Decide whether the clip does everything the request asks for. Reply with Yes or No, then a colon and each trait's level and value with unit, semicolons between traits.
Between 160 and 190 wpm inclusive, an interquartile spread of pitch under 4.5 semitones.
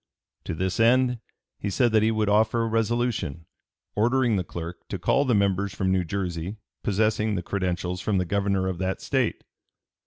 Yes: average, 180 wpm; average, 3.4 semitones